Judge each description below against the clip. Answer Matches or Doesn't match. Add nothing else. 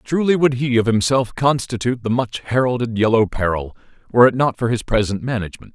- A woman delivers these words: Doesn't match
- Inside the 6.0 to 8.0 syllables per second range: Matches